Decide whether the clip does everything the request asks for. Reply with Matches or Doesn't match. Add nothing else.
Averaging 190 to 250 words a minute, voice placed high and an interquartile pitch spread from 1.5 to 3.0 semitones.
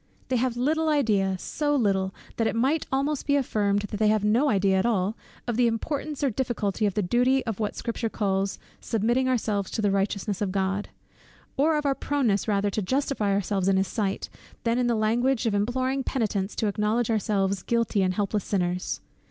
Doesn't match